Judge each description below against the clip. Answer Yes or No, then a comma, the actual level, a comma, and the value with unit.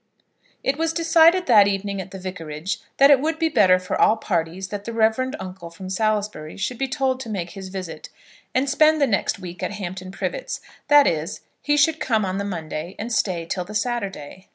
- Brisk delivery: Yes, fast, 210 wpm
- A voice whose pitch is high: Yes, high, 200 Hz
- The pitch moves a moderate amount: No, wide, 6.1 semitones